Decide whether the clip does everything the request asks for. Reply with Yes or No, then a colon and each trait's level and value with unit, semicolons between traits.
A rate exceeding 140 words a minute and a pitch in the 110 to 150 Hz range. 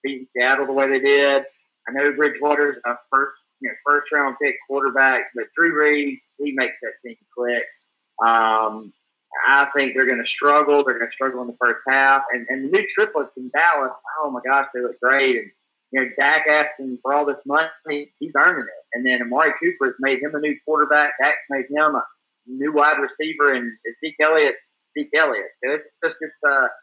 Yes: fast, 205 wpm; medium, 140 Hz